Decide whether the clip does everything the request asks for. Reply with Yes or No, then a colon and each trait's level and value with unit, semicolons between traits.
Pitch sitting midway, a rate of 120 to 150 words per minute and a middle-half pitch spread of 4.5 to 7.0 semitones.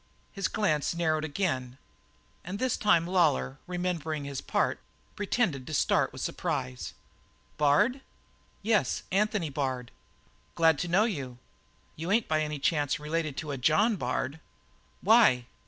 Yes: medium, 160 Hz; slow, 135 wpm; wide, 5.5 semitones